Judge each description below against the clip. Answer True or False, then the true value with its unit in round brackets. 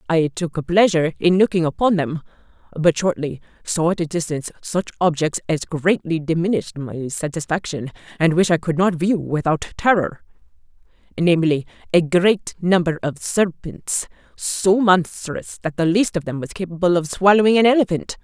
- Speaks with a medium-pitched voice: True (170 Hz)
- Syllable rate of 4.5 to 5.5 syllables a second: True (5.0 syllables/s)